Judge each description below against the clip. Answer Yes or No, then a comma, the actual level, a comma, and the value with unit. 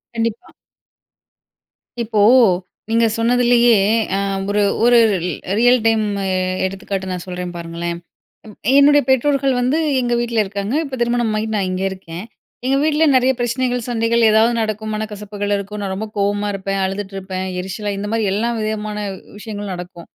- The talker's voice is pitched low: No, high, 215 Hz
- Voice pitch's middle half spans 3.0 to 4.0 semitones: Yes, average, 3.3 semitones